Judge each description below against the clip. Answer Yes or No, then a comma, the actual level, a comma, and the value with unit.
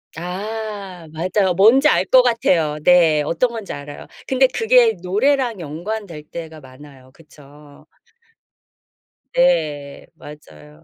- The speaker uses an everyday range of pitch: No, wide, 6.9 semitones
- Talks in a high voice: No, medium, 175 Hz